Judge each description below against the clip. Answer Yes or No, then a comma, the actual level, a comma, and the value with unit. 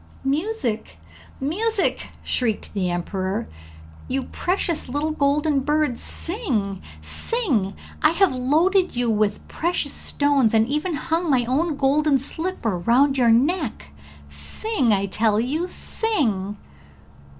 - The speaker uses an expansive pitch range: Yes, wide, 6.7 semitones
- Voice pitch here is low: No, very high, 275 Hz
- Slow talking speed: Yes, slow, 115 wpm